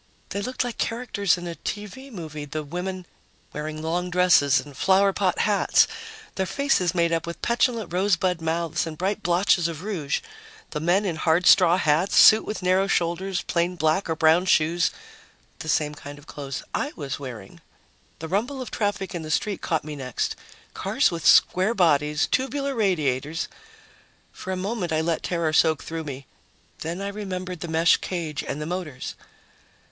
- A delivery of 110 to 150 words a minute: No, average, 175 wpm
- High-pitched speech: No, medium, 175 Hz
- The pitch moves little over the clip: No, average, 3.7 semitones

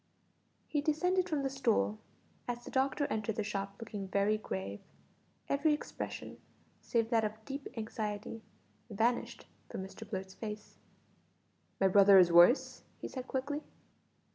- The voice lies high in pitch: Yes, high, 220 Hz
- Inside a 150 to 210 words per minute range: No, average, 140 wpm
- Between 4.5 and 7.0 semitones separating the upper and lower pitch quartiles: Yes, average, 5.1 semitones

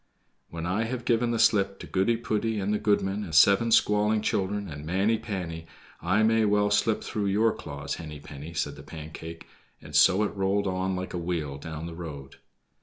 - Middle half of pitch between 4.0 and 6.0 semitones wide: Yes, average, 4.4 semitones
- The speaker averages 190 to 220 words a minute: Yes, average, 195 wpm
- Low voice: Yes, very low, 95 Hz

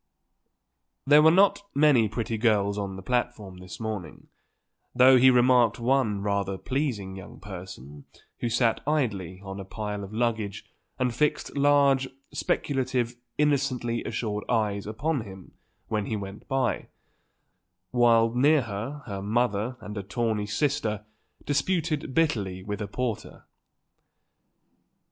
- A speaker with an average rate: No, slow, 130 wpm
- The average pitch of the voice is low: Yes, low, 115 Hz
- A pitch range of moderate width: Yes, average, 4.5 semitones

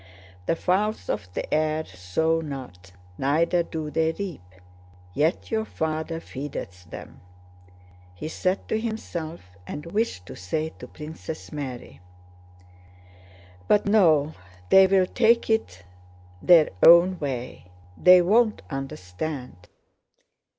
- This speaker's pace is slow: Yes, slow, 115 wpm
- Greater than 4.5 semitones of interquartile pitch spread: Yes, average, 5.3 semitones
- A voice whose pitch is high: No, medium, 160 Hz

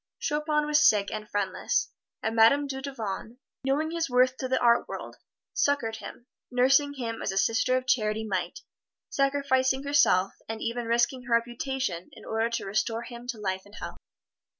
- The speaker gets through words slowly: No, average, 170 wpm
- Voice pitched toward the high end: Yes, high, 240 Hz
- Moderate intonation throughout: Yes, average, 3.5 semitones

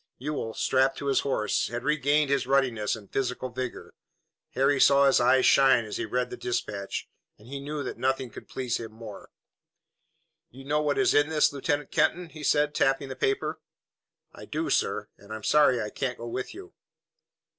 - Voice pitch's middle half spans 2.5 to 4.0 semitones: Yes, average, 3.1 semitones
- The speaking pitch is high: No, low, 135 Hz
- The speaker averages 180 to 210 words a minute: Yes, average, 190 wpm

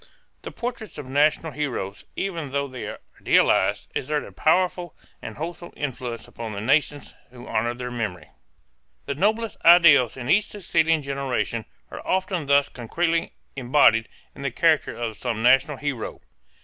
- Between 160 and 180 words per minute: No, average, 150 wpm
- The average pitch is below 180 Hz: Yes, medium, 140 Hz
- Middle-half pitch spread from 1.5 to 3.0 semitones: No, average, 5.3 semitones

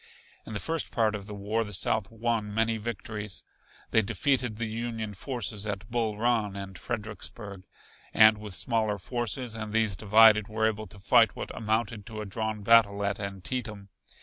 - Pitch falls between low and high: No, low, 110 Hz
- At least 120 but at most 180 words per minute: Yes, average, 175 wpm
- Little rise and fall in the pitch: Yes, narrow, 1.8 semitones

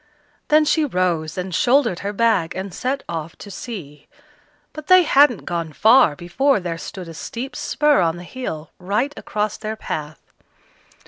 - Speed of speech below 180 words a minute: Yes, average, 165 wpm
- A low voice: No, high, 200 Hz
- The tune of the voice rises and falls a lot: Yes, wide, 7.6 semitones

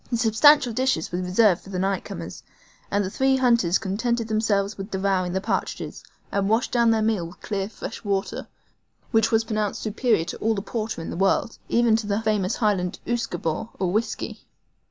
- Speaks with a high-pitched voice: Yes, high, 215 Hz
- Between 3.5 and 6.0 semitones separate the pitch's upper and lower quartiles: No, average, 3.0 semitones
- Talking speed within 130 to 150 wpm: No, average, 190 wpm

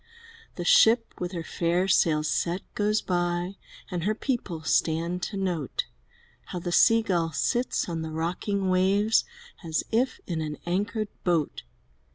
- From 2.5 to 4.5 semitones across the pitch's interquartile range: Yes, average, 3.5 semitones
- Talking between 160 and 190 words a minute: No, average, 150 wpm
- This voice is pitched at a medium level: Yes, medium, 180 Hz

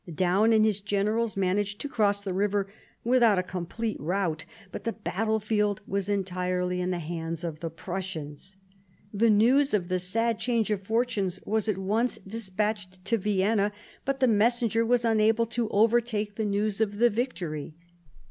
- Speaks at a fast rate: No, average, 165 wpm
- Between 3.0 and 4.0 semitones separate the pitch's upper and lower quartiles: Yes, average, 3.4 semitones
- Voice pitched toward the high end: Yes, high, 205 Hz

